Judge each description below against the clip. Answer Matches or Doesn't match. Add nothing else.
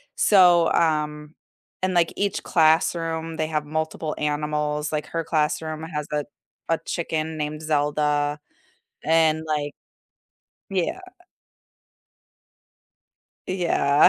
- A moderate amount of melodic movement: Doesn't match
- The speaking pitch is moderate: Matches